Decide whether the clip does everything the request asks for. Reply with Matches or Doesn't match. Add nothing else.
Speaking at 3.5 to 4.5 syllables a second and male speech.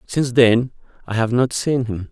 Doesn't match